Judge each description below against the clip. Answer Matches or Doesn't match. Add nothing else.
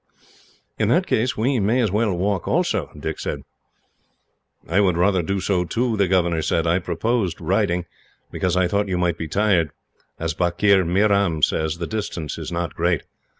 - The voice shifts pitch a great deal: Doesn't match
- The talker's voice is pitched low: Matches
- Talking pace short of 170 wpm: Doesn't match